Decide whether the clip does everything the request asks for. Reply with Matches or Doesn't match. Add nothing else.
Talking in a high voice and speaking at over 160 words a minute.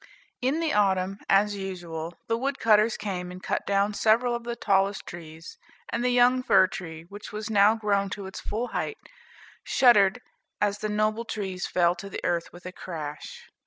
Matches